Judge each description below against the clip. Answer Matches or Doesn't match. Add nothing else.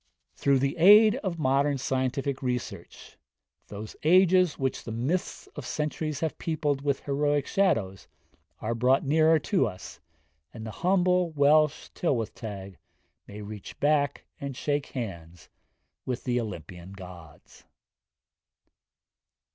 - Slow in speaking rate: Matches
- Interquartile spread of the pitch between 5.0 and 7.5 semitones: Matches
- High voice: Doesn't match